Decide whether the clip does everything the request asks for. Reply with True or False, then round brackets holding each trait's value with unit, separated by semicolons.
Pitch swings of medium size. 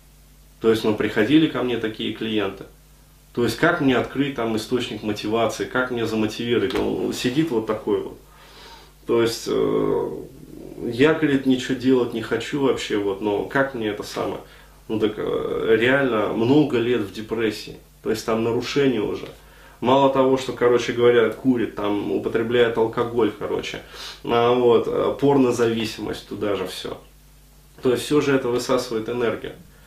True (3.0 semitones)